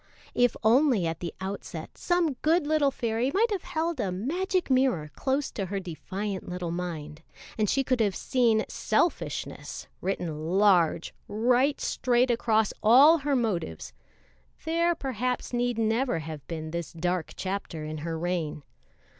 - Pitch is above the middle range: Yes, high, 220 Hz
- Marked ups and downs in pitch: Yes, wide, 7.4 semitones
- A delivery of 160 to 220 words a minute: No, average, 145 wpm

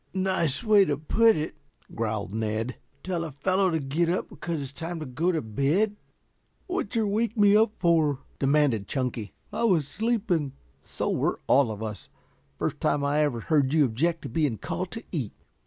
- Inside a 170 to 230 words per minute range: Yes, average, 180 wpm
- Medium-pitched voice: Yes, medium, 155 Hz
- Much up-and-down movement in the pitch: Yes, wide, 6.0 semitones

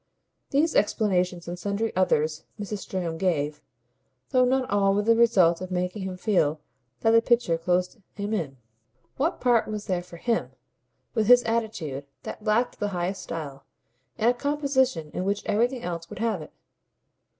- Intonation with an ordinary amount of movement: Yes, average, 4.8 semitones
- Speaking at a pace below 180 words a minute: Yes, average, 165 wpm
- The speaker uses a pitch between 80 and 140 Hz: No, high, 200 Hz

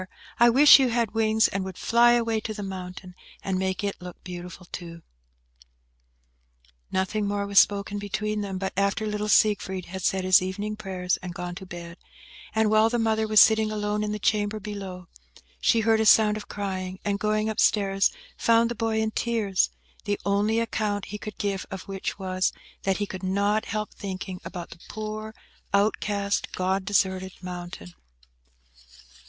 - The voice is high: Yes, high, 205 Hz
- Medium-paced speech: Yes, average, 175 wpm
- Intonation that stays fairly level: Yes, narrow, 2.3 semitones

